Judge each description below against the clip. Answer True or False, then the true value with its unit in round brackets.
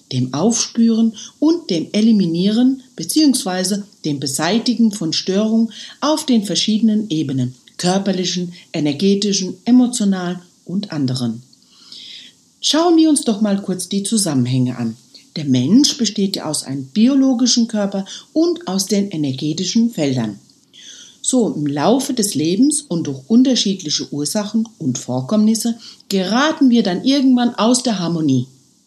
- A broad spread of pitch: True (7.0 semitones)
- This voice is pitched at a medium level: False (200 Hz)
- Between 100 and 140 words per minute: True (125 wpm)